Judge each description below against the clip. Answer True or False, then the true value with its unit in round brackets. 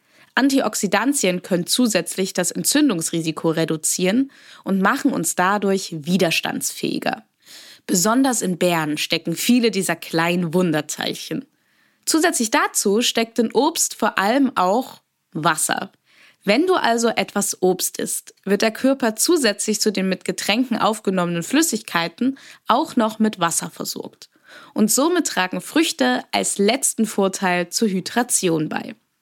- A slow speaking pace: True (120 wpm)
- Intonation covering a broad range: True (5.9 semitones)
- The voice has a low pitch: False (205 Hz)